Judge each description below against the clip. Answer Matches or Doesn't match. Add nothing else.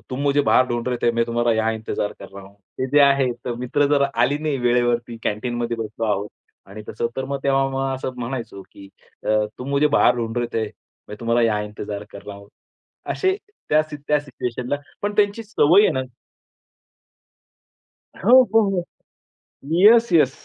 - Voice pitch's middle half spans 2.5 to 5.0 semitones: Matches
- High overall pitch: Doesn't match